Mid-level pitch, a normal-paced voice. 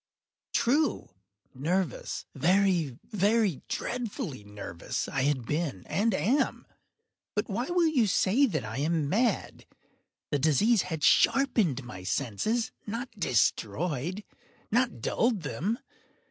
No: medium, 180 Hz; slow, 100 wpm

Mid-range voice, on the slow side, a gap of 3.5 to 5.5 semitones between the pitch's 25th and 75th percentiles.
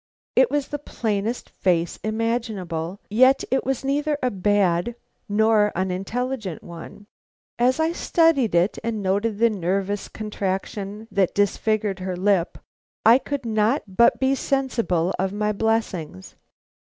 No: high, 210 Hz; slow, 130 wpm; average, 4.2 semitones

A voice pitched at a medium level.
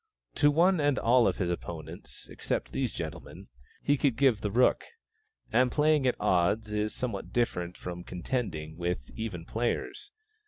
No: low, 110 Hz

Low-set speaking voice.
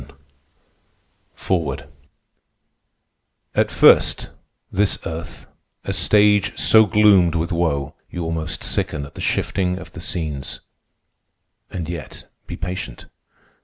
Yes: very low, 85 Hz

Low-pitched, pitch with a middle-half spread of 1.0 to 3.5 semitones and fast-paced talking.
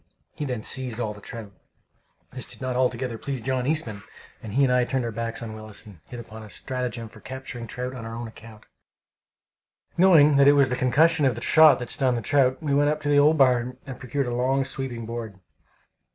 Yes: low, 125 Hz; average, 2.9 semitones; fast, 225 wpm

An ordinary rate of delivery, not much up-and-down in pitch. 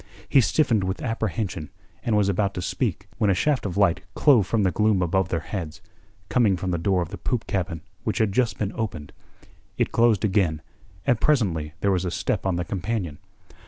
No: average, 195 wpm; average, 3.8 semitones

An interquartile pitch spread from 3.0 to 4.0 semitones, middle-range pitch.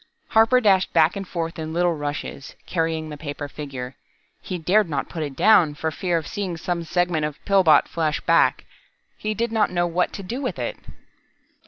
Yes: average, 3.7 semitones; medium, 170 Hz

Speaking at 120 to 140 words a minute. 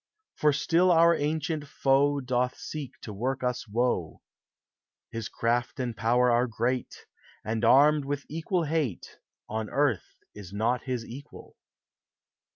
Yes: slow, 135 wpm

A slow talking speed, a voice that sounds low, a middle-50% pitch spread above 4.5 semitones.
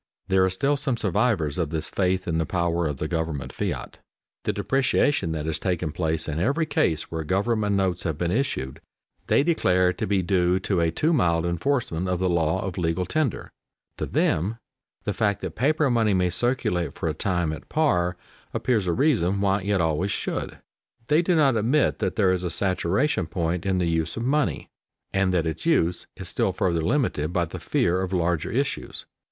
No: average, 195 wpm; very low, 90 Hz; average, 5.2 semitones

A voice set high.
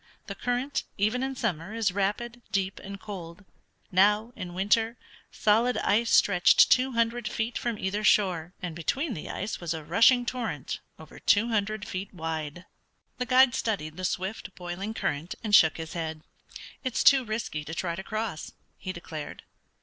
Yes: high, 200 Hz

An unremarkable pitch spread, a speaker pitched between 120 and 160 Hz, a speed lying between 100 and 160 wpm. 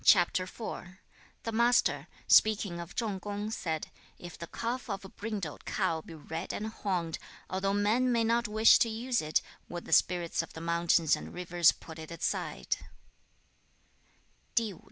No: average, 4.5 semitones; high, 190 Hz; average, 150 wpm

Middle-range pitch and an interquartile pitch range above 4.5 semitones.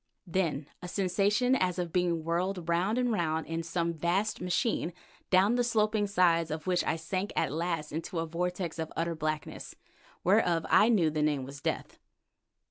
No: medium, 175 Hz; average, 3.1 semitones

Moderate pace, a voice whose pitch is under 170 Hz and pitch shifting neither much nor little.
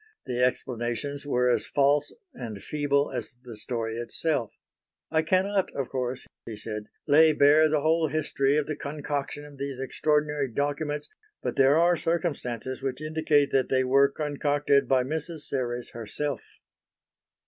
Yes: average, 150 wpm; medium, 140 Hz; average, 3.0 semitones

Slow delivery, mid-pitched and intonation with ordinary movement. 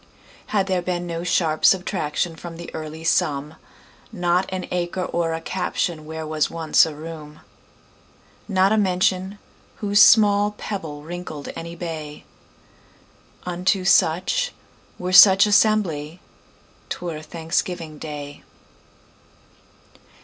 Yes: slow, 95 wpm; medium, 175 Hz; average, 3.0 semitones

